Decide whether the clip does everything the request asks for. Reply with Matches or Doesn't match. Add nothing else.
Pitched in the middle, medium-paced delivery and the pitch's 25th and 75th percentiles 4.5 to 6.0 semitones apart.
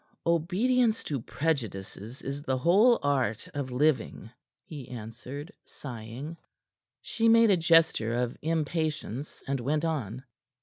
Doesn't match